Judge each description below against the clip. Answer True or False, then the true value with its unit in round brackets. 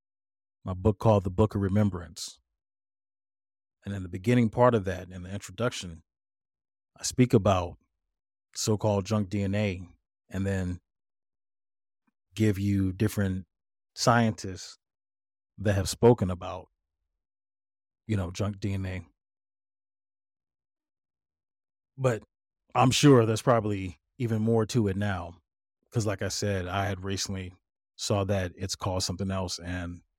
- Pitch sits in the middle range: False (100 Hz)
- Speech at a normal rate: False (125 wpm)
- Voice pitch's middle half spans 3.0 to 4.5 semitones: False (2.5 semitones)